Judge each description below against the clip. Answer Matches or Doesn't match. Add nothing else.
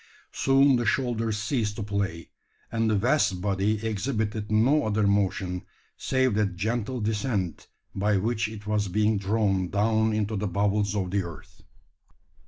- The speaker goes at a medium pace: Matches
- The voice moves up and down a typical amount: Doesn't match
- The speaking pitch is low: Matches